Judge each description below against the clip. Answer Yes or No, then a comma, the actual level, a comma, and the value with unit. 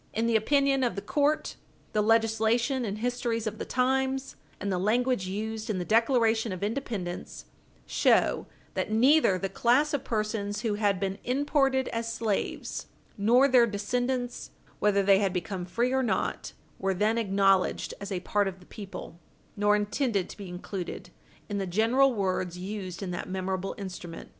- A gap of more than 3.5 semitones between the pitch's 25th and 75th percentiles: Yes, average, 4.0 semitones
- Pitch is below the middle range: No, high, 215 Hz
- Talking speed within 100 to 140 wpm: No, average, 165 wpm